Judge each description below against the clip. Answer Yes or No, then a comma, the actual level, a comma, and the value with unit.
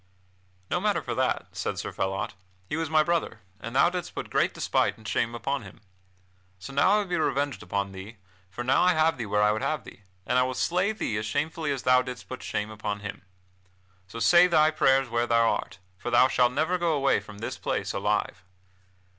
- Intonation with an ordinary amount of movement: No, wide, 6.4 semitones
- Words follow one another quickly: Yes, fast, 220 wpm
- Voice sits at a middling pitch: No, low, 130 Hz